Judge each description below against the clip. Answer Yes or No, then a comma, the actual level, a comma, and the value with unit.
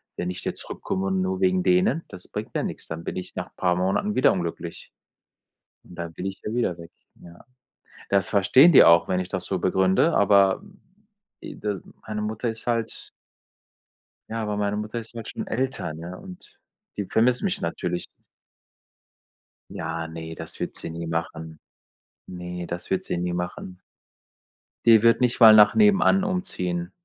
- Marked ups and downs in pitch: Yes, wide, 5.7 semitones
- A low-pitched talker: Yes, low, 100 Hz